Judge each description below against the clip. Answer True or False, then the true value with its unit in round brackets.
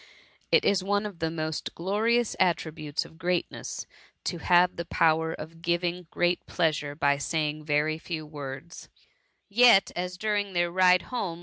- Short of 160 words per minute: True (150 wpm)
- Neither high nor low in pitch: True (170 Hz)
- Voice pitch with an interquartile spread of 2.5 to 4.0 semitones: True (2.8 semitones)